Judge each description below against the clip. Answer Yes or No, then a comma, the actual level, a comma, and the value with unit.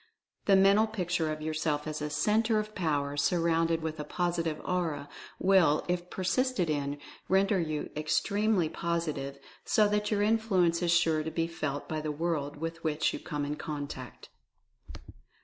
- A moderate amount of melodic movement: Yes, average, 3.7 semitones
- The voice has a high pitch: No, medium, 165 Hz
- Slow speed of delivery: No, average, 160 wpm